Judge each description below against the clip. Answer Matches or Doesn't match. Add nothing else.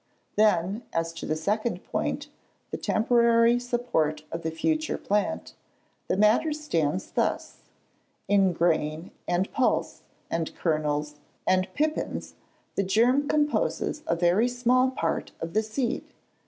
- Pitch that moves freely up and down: Matches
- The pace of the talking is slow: Matches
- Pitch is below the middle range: Doesn't match